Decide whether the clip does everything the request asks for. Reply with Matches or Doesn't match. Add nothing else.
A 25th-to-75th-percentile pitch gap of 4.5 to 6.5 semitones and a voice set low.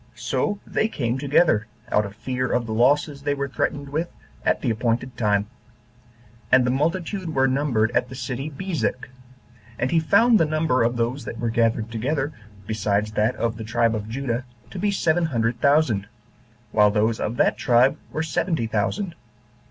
Matches